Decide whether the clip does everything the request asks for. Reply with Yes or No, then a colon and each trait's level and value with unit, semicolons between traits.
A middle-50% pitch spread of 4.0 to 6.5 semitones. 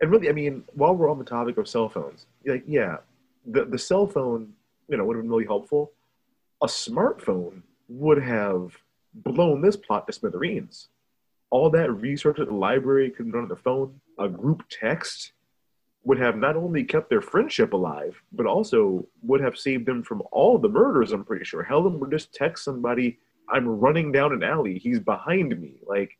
Yes: average, 4.4 semitones